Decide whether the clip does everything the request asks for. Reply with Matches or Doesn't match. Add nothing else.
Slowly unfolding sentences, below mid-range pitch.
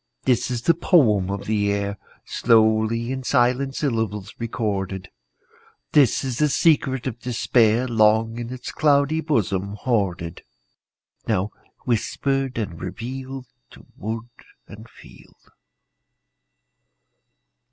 Matches